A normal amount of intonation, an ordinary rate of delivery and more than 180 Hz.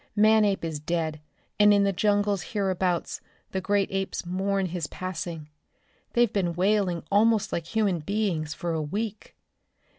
Yes: average, 3.2 semitones; average, 145 wpm; high, 190 Hz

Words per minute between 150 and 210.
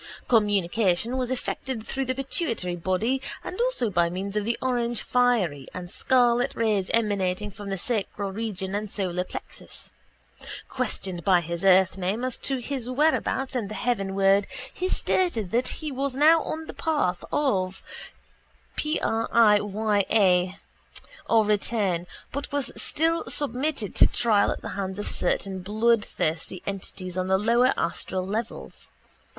No: slow, 135 wpm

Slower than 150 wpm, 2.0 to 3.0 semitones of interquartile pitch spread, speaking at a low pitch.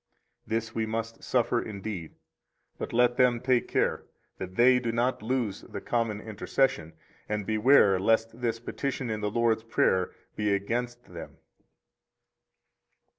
Yes: slow, 135 wpm; narrow, 2.4 semitones; low, 115 Hz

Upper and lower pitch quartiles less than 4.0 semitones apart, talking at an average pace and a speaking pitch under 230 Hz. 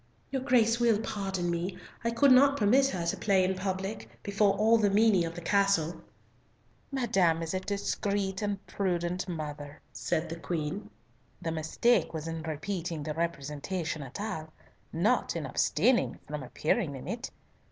No: average, 4.3 semitones; average, 160 wpm; high, 190 Hz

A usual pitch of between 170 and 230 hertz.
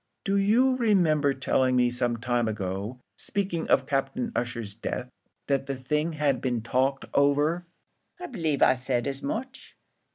No: medium, 140 Hz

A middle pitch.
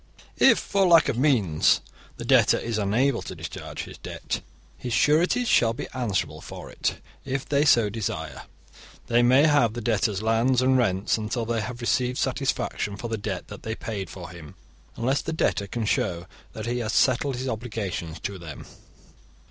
No: low, 115 Hz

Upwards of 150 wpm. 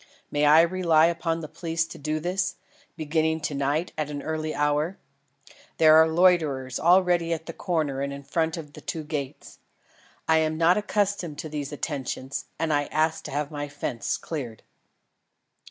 Yes: average, 170 wpm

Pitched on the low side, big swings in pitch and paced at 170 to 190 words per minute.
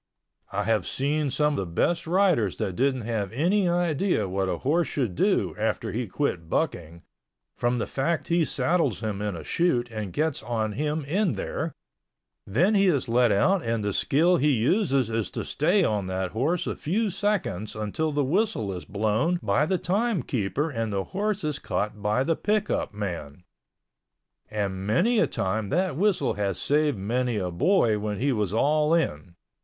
Yes: low, 125 Hz; wide, 8.4 semitones; average, 180 wpm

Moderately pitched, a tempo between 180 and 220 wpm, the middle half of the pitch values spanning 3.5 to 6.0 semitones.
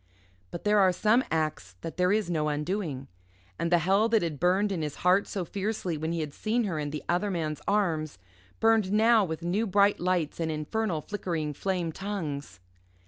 Yes: medium, 180 Hz; average, 195 wpm; average, 4.6 semitones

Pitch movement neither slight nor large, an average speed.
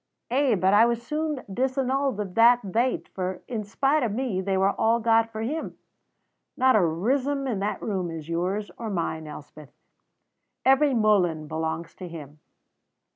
No: wide, 6.0 semitones; average, 165 wpm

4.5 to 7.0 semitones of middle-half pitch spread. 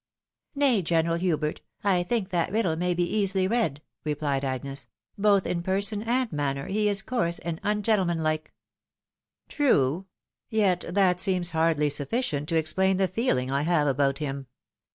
Yes: average, 4.9 semitones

